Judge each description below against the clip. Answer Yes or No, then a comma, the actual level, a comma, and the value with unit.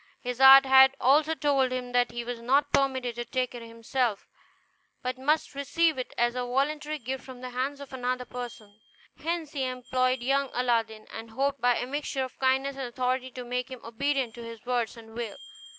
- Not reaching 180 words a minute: No, average, 200 wpm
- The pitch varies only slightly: Yes, narrow, 2.0 semitones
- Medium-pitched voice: No, very high, 255 Hz